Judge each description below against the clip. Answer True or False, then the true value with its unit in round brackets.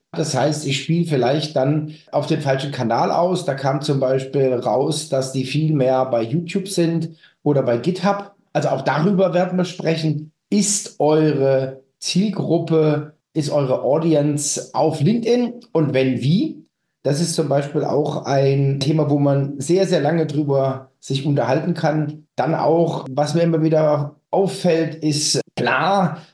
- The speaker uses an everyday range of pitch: True (3.2 semitones)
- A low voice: False (150 Hz)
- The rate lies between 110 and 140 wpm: False (155 wpm)